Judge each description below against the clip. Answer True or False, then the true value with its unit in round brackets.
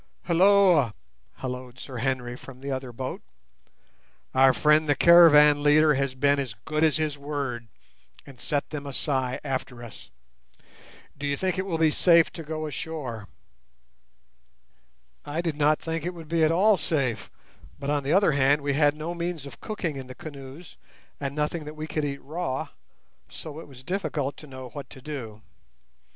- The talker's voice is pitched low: False (145 Hz)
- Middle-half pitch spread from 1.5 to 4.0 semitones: True (3.2 semitones)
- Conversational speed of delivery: True (175 wpm)